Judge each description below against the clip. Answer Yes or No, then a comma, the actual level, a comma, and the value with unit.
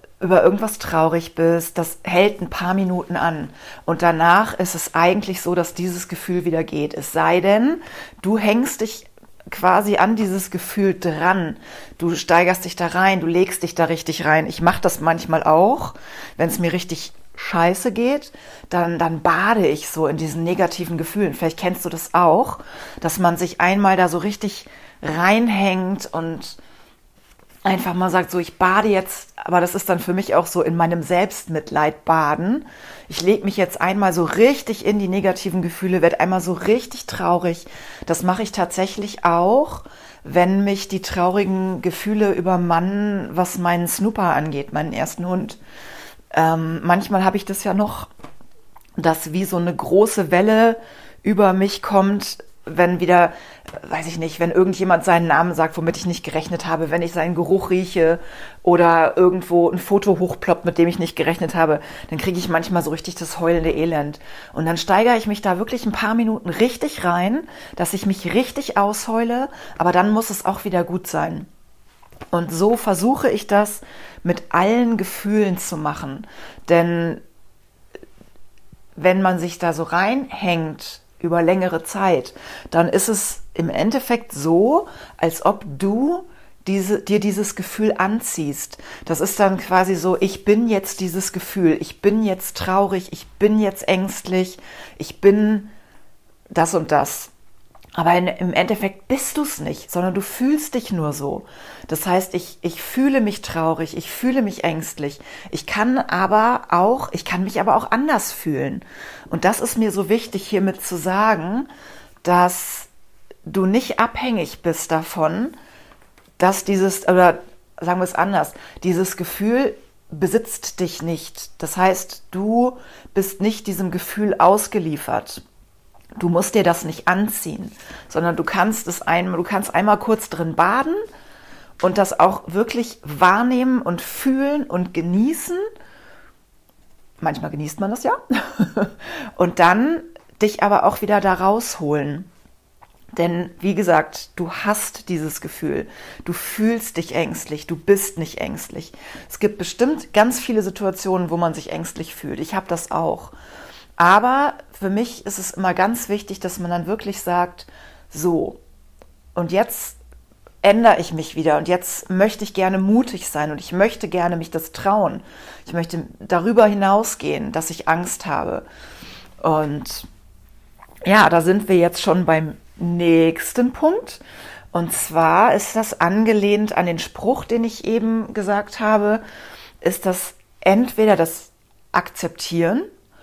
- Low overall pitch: No, medium, 185 Hz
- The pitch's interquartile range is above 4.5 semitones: No, average, 3.5 semitones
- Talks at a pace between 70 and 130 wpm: No, average, 155 wpm